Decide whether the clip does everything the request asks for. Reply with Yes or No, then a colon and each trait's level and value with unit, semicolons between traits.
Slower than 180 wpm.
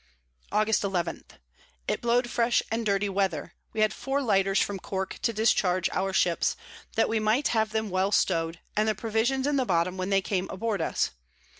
No: average, 185 wpm